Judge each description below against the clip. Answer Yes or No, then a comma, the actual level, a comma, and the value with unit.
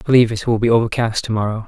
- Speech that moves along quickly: Yes, fast, 285 wpm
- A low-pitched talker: Yes, low, 115 Hz